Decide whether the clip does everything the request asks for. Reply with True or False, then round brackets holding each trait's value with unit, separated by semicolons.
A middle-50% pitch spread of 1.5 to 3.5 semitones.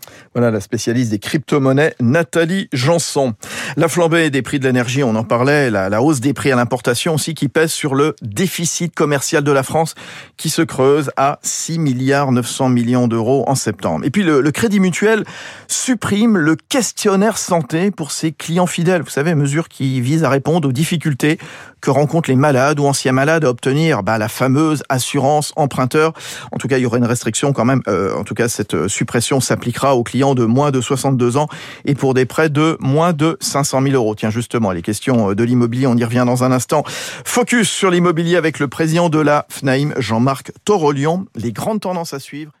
False (4.2 semitones)